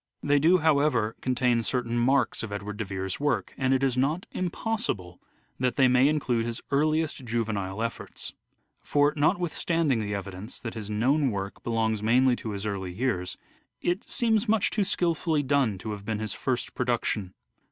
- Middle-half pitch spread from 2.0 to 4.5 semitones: No, wide, 5.4 semitones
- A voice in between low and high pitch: No, low, 125 Hz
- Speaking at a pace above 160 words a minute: Yes, average, 170 wpm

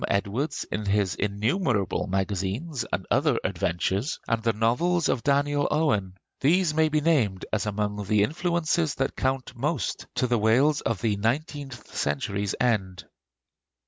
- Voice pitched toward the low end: Yes, low, 115 Hz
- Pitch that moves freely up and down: Yes, wide, 6.3 semitones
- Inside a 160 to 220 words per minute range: No, average, 145 wpm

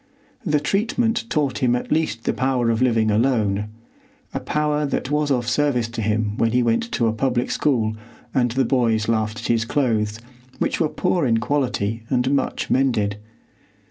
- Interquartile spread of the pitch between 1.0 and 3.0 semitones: No, average, 4.2 semitones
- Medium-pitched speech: No, low, 125 Hz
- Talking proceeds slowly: No, average, 175 wpm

